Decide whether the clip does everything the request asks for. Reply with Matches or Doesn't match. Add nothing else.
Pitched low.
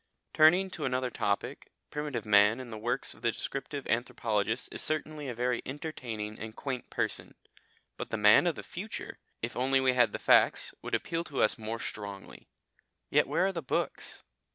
Matches